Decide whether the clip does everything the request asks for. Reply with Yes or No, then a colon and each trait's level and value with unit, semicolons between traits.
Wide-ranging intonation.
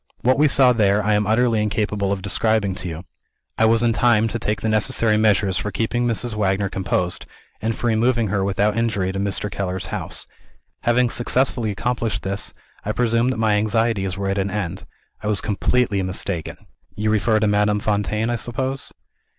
No: average, 2.7 semitones